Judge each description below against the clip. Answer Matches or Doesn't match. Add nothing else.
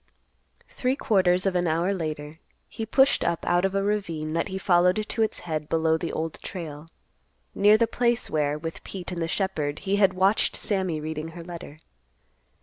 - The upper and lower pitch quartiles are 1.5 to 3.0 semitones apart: Doesn't match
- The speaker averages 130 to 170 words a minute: Doesn't match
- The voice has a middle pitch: Matches